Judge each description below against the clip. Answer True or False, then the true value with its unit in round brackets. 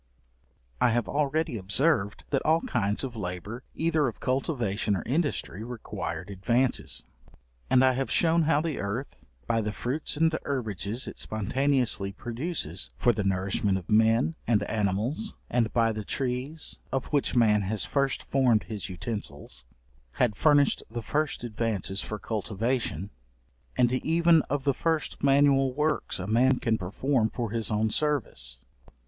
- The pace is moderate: True (150 wpm)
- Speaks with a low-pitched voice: True (120 Hz)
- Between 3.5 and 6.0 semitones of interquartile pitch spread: True (4.9 semitones)